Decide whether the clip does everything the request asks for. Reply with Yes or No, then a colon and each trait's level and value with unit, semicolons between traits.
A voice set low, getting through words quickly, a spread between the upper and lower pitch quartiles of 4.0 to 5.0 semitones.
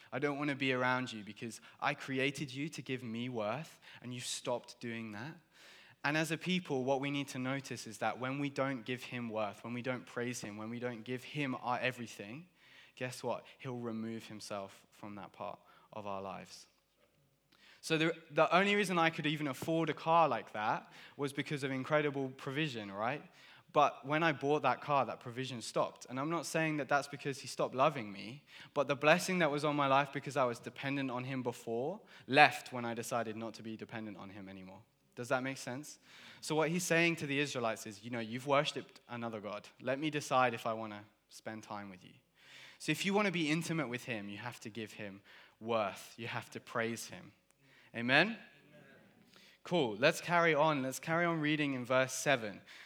Yes: low, 130 Hz; fast, 210 wpm; average, 4.3 semitones